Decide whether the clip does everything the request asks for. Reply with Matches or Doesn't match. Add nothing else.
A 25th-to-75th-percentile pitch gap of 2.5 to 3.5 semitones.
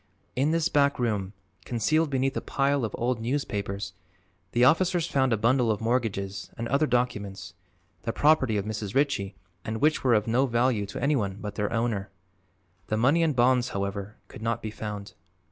Doesn't match